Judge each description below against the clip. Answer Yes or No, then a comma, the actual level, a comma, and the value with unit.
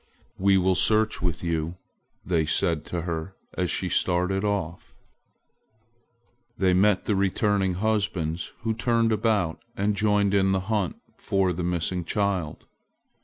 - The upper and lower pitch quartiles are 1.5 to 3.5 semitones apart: Yes, average, 2.8 semitones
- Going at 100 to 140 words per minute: Yes, slow, 135 wpm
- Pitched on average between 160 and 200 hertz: No, very low, 95 Hz